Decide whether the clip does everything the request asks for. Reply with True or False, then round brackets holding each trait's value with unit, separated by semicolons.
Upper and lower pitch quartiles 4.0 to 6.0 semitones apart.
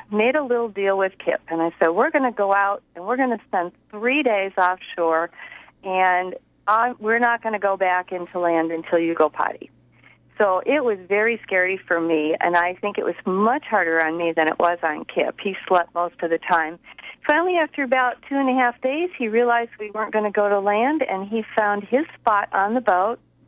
True (5.2 semitones)